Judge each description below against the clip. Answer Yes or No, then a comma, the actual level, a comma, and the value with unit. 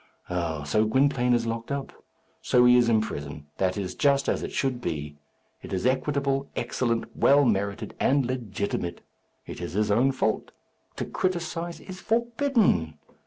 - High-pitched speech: No, low, 120 Hz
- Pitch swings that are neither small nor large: No, wide, 5.9 semitones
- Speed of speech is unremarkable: Yes, average, 160 wpm